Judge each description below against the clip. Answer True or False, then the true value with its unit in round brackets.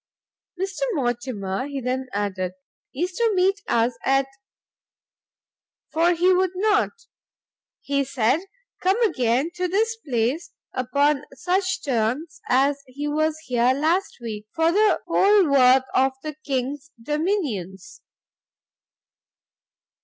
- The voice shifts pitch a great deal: True (6.3 semitones)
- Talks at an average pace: False (115 wpm)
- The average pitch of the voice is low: False (285 Hz)